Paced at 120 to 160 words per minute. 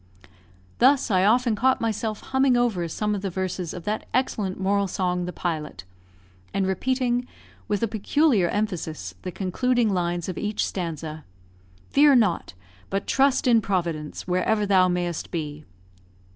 Yes: average, 145 wpm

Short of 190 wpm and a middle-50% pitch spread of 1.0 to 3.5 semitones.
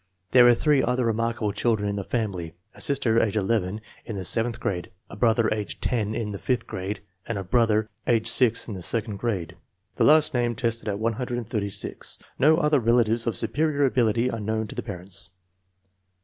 No: average, 195 wpm; average, 2.8 semitones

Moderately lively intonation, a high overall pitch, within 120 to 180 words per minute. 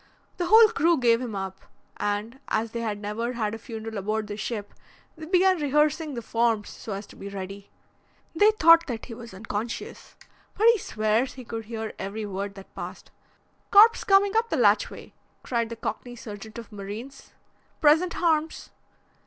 No: wide, 6.9 semitones; high, 230 Hz; average, 175 wpm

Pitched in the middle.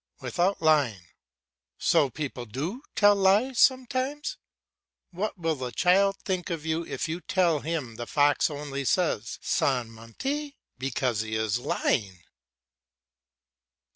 Yes: medium, 155 Hz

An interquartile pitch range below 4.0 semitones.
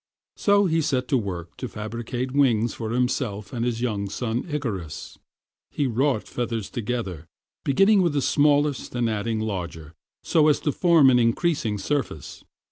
No: average, 5.0 semitones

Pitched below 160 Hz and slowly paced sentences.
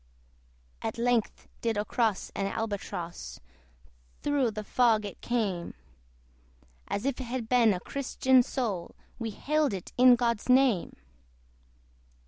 No: high, 235 Hz; slow, 120 wpm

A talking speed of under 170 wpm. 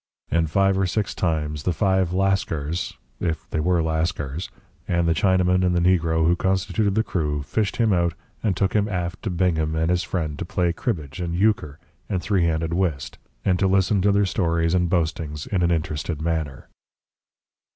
No: average, 185 wpm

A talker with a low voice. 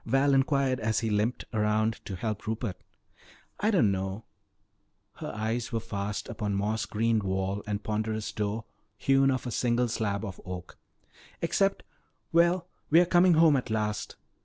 Yes: low, 110 Hz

